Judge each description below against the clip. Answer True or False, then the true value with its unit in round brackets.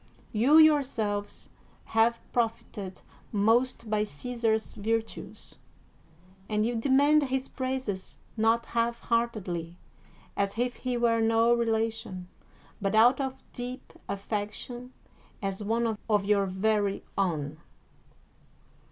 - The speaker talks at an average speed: False (110 wpm)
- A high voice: True (225 Hz)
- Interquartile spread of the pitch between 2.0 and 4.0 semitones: True (2.9 semitones)